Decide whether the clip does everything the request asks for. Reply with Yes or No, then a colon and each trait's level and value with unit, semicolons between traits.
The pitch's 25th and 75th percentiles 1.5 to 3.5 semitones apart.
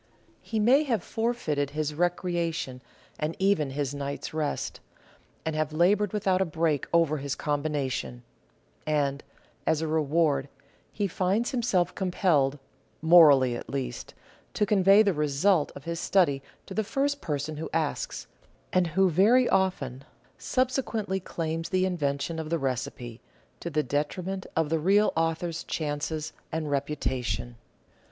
No: average, 4.7 semitones